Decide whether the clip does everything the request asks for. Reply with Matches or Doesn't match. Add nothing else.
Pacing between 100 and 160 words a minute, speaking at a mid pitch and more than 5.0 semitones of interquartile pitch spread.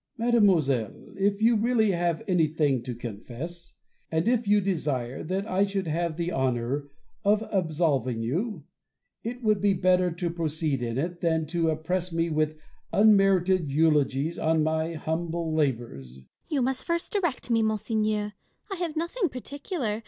Matches